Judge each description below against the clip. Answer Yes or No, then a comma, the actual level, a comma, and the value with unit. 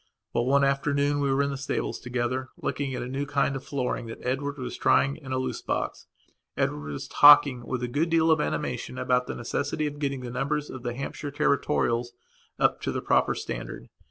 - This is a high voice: No, low, 135 Hz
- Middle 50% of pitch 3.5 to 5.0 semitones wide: No, narrow, 2.5 semitones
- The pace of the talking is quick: Yes, fast, 210 wpm